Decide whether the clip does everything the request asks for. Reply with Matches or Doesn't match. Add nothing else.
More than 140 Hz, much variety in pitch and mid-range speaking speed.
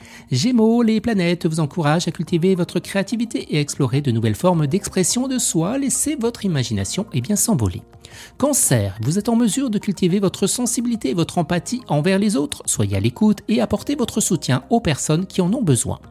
Matches